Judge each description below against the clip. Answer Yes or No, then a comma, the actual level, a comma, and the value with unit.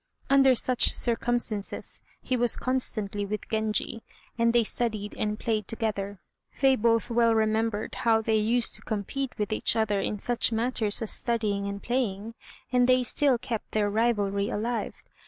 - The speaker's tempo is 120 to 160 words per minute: Yes, average, 155 wpm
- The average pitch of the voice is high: Yes, high, 225 Hz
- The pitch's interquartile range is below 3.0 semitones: Yes, narrow, 2.4 semitones